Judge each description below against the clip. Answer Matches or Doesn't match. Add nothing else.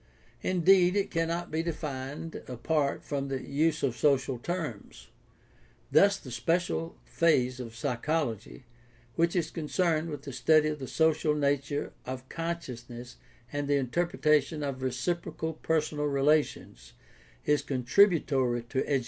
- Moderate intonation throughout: Matches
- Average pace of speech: Doesn't match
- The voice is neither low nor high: Matches